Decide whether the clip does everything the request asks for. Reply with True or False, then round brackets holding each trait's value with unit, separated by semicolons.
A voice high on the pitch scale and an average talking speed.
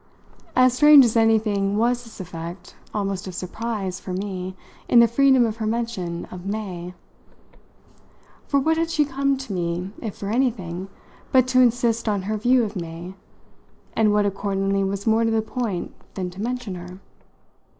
True (210 Hz; 170 wpm)